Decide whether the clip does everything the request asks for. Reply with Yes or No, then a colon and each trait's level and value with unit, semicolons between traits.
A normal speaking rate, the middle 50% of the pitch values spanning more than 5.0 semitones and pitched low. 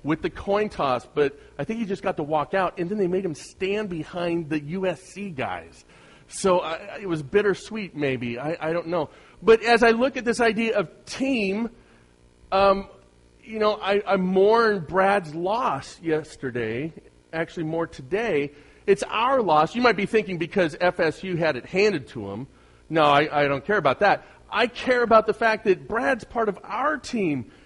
No: average, 185 wpm; wide, 5.4 semitones; medium, 185 Hz